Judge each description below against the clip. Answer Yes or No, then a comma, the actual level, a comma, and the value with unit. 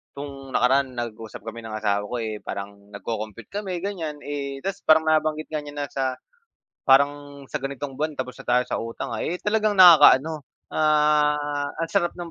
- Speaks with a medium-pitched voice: Yes, medium, 145 Hz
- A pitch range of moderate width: Yes, average, 4.1 semitones